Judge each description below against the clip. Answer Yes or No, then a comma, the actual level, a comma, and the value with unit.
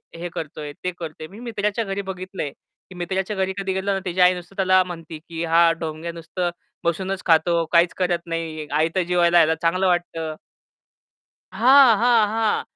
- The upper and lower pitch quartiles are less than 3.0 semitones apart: Yes, narrow, 2.6 semitones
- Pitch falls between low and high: Yes, medium, 180 Hz